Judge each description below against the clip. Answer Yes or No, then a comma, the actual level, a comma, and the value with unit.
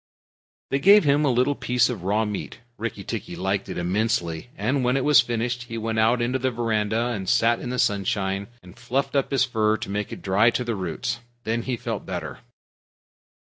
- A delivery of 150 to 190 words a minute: No, fast, 205 wpm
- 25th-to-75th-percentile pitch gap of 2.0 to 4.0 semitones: Yes, average, 3.2 semitones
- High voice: No, low, 115 Hz